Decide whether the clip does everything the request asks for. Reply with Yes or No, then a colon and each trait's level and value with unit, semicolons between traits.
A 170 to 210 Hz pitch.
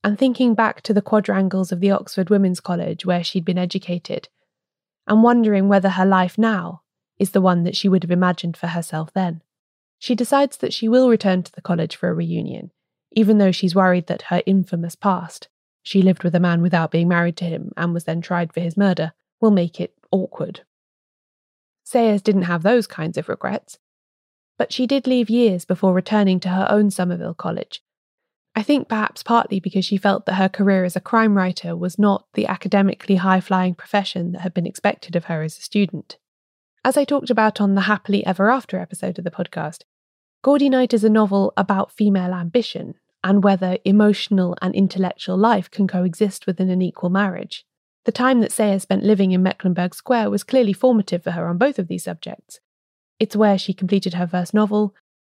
Yes: high, 190 Hz